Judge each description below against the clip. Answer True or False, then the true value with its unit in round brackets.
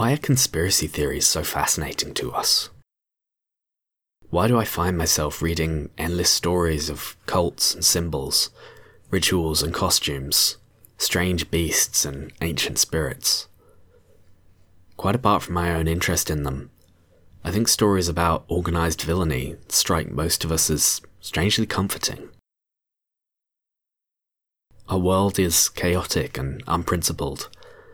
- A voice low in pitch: True (85 Hz)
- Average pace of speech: False (120 wpm)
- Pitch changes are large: False (2.6 semitones)